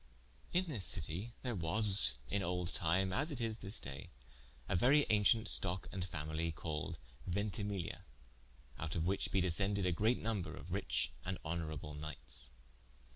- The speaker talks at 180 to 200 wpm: No, average, 160 wpm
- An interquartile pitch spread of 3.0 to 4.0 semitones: No, average, 4.6 semitones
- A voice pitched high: No, very low, 95 Hz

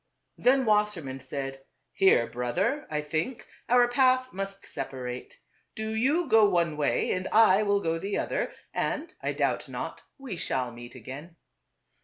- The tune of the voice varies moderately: No, wide, 8.8 semitones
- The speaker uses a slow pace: No, average, 150 wpm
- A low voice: No, high, 195 Hz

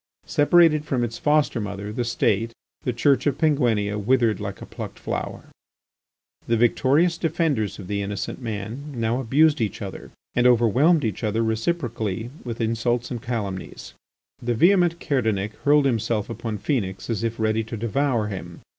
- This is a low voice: Yes, low, 115 Hz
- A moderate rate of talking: Yes, average, 155 wpm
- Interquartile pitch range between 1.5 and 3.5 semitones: No, average, 4.5 semitones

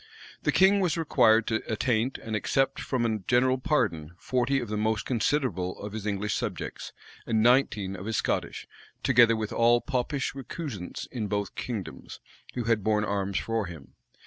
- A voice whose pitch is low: Yes, low, 115 Hz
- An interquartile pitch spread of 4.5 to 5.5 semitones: No, average, 3.7 semitones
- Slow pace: No, average, 170 wpm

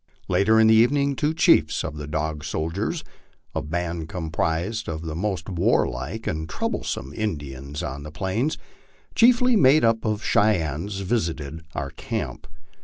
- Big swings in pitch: Yes, wide, 6.2 semitones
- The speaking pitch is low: Yes, very low, 85 Hz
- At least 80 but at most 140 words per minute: No, average, 150 wpm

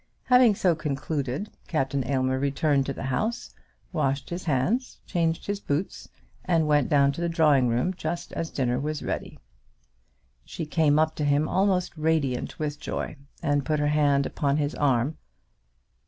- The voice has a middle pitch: Yes, medium, 150 Hz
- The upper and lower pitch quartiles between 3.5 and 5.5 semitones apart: No, average, 3.0 semitones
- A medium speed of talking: Yes, average, 160 wpm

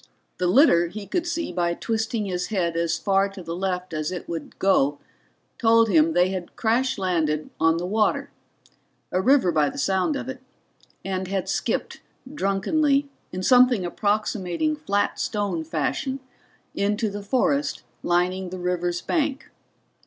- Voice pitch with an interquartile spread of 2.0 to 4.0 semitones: No, average, 4.5 semitones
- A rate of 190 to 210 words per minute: No, average, 155 wpm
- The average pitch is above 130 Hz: Yes, high, 190 Hz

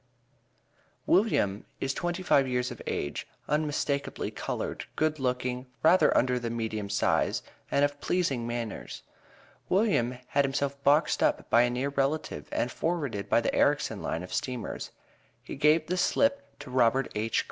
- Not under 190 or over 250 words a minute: No, average, 150 wpm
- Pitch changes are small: No, average, 4.2 semitones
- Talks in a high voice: No, low, 135 Hz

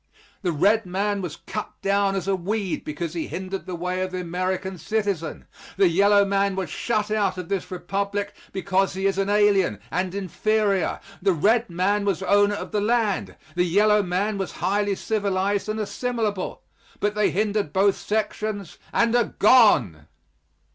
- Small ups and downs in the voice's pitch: Yes, narrow, 2.1 semitones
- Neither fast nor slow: Yes, average, 170 wpm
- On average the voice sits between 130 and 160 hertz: No, high, 195 Hz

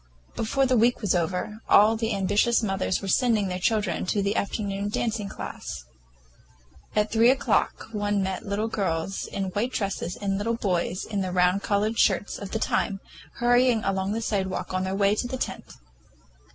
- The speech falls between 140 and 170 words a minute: No, average, 180 wpm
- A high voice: Yes, high, 205 Hz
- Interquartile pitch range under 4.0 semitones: Yes, narrow, 2.6 semitones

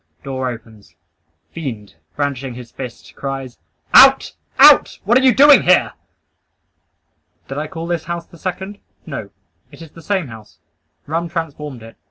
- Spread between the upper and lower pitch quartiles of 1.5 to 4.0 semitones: No, average, 5.3 semitones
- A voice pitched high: No, medium, 150 Hz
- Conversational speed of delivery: Yes, average, 150 wpm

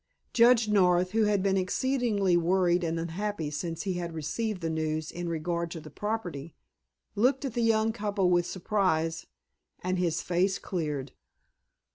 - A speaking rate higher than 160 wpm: No, average, 155 wpm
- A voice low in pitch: No, medium, 180 Hz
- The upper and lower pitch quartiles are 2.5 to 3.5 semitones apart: No, average, 4.0 semitones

